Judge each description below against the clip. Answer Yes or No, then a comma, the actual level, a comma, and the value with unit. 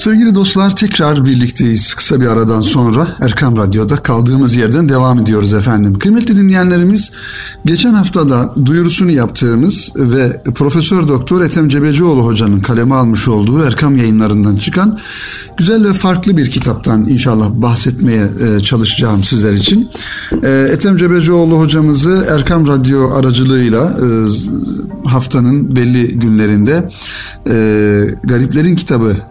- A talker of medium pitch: No, low, 130 Hz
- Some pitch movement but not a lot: No, wide, 7.0 semitones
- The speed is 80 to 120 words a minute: Yes, average, 110 wpm